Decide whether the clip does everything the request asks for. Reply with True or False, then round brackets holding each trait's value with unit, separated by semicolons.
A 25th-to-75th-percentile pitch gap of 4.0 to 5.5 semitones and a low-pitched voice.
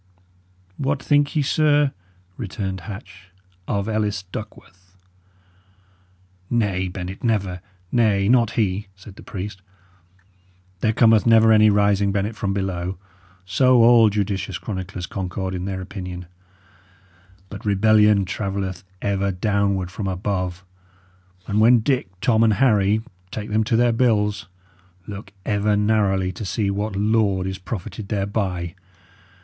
False (2.6 semitones; 100 Hz)